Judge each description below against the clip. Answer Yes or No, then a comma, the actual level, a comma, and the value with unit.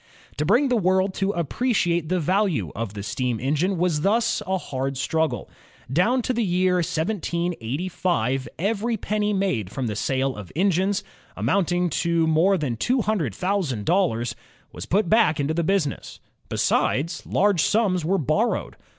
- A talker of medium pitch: Yes, medium, 175 Hz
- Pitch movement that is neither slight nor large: No, wide, 5.9 semitones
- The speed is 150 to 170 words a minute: Yes, average, 155 wpm